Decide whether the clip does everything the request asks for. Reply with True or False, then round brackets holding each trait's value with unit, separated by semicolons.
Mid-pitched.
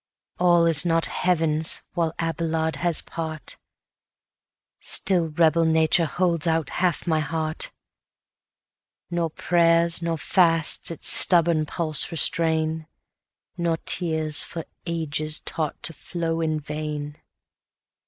True (165 Hz)